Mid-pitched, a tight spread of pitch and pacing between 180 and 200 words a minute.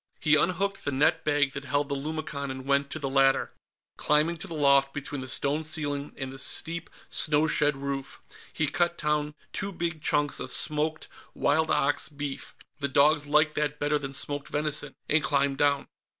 Yes: medium, 145 Hz; narrow, 1.7 semitones; average, 185 wpm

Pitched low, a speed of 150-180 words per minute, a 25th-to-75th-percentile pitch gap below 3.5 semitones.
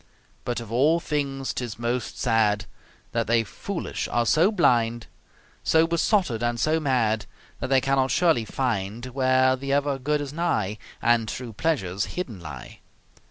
No: low, 125 Hz; average, 155 wpm; average, 4.2 semitones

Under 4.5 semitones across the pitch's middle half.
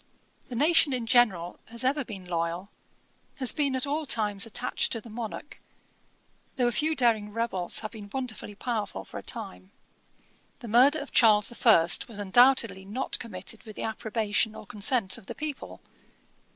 Yes: average, 3.9 semitones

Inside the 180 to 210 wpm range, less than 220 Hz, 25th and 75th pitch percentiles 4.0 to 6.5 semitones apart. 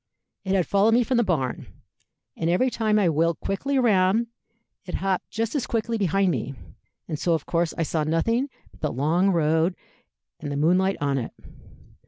Yes: average, 185 wpm; medium, 185 Hz; average, 5.1 semitones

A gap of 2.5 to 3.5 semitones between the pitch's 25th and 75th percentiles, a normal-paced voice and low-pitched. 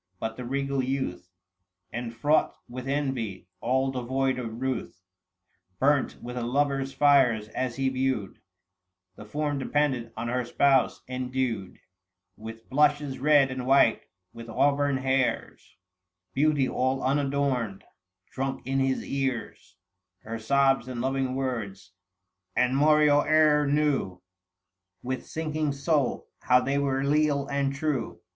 No: average, 2.8 semitones; slow, 130 wpm; low, 130 Hz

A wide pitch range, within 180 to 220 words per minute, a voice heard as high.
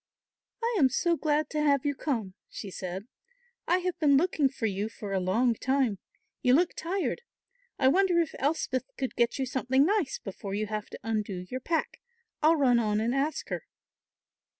Yes: wide, 6.0 semitones; average, 185 wpm; very high, 265 Hz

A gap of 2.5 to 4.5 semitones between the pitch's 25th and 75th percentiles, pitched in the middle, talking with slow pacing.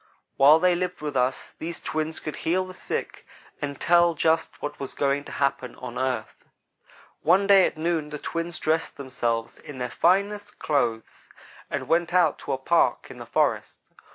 No: average, 3.9 semitones; medium, 155 Hz; average, 180 wpm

